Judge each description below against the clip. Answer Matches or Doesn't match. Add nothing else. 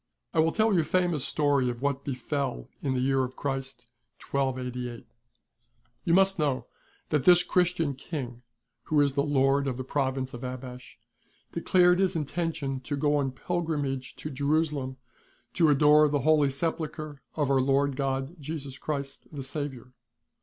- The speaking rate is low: Doesn't match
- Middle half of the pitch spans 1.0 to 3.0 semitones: Matches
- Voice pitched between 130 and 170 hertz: Matches